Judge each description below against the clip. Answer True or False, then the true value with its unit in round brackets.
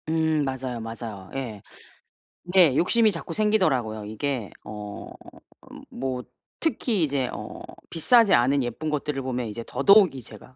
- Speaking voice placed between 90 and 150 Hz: True (135 Hz)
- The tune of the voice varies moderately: False (5.9 semitones)